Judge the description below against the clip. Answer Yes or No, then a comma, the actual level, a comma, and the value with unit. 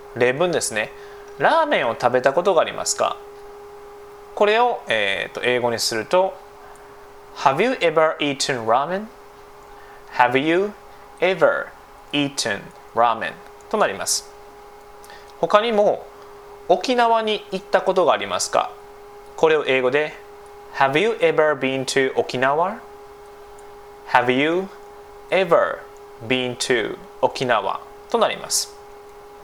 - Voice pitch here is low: No, high, 205 Hz